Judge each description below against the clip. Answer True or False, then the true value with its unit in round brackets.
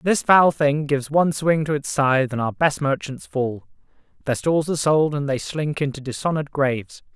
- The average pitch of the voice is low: False (145 Hz)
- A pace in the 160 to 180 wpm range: False (200 wpm)